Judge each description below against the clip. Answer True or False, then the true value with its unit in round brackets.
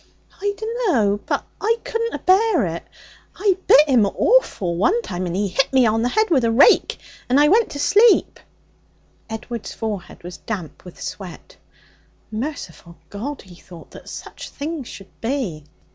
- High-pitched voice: True (245 Hz)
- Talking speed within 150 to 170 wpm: True (160 wpm)